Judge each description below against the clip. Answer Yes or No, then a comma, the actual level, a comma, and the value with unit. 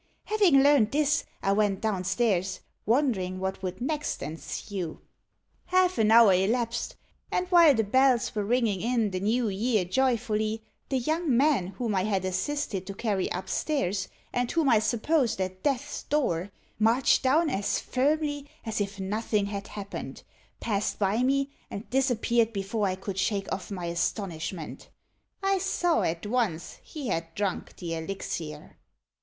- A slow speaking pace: No, average, 155 wpm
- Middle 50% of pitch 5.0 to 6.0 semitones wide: Yes, wide, 5.6 semitones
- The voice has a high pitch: Yes, high, 220 Hz